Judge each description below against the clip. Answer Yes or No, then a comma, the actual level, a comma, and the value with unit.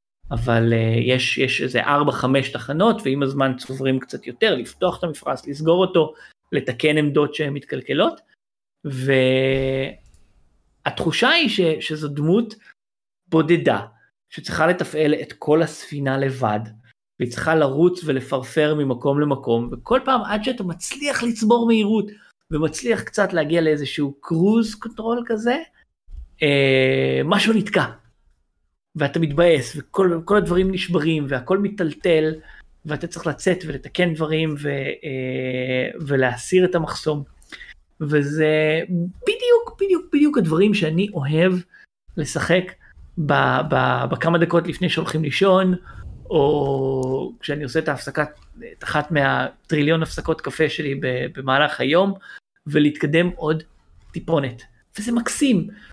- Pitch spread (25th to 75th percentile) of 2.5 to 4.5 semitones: No, average, 5.0 semitones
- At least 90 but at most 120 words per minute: Yes, average, 110 wpm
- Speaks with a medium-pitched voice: Yes, medium, 155 Hz